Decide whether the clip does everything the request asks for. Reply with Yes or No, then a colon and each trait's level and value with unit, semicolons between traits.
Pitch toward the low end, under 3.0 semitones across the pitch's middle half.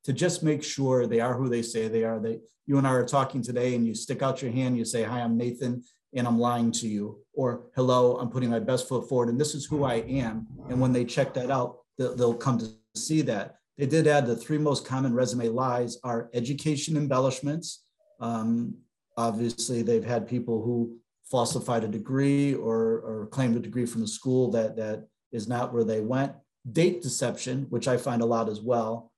Yes: low, 125 Hz; narrow, 2.4 semitones